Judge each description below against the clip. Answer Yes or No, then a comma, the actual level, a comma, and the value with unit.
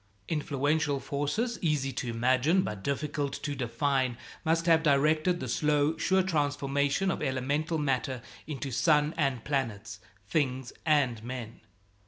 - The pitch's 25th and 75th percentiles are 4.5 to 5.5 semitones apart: No, average, 3.0 semitones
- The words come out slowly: Yes, slow, 130 wpm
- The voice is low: No, medium, 145 Hz